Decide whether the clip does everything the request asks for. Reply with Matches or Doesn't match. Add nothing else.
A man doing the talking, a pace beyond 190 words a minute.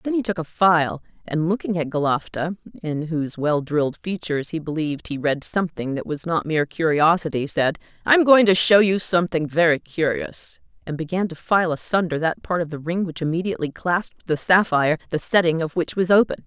Doesn't match